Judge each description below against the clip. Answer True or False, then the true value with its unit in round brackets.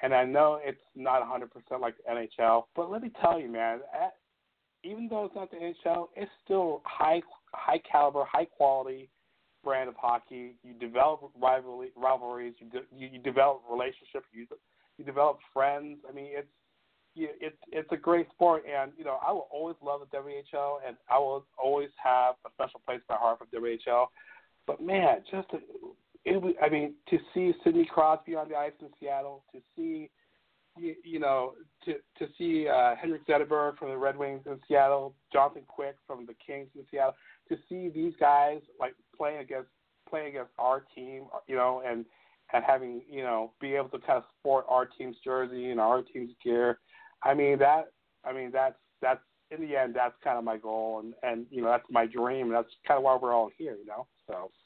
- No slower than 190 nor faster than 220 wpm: True (200 wpm)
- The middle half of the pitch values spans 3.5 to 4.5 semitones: True (4.0 semitones)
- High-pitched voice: False (140 Hz)